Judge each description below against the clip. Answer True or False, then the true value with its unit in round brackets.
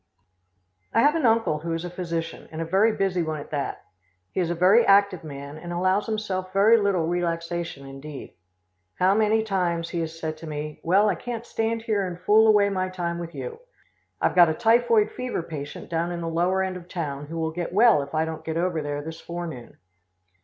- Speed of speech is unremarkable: False (215 wpm)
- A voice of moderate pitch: True (175 Hz)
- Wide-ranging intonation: False (3.8 semitones)